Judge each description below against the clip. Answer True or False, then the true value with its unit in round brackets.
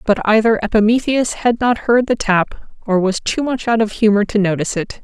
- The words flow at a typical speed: False (215 wpm)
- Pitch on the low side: False (215 Hz)